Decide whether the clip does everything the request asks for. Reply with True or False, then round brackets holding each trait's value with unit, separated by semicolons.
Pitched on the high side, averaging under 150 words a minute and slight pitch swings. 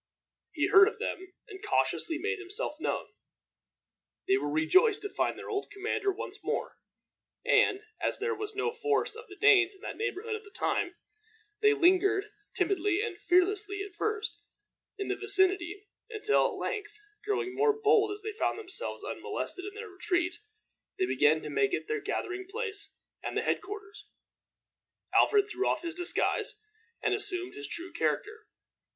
False (405 Hz; 165 wpm; 2.3 semitones)